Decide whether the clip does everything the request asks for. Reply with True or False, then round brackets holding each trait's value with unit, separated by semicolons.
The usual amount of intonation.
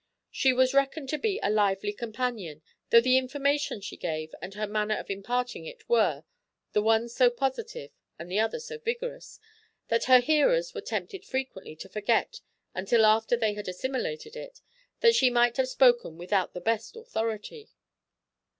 False (6.5 semitones)